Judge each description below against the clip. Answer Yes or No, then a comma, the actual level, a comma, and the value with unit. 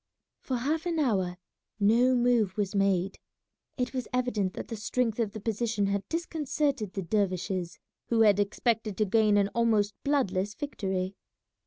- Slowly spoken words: No, average, 155 wpm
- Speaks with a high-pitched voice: Yes, high, 215 Hz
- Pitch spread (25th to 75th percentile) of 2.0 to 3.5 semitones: No, average, 3.9 semitones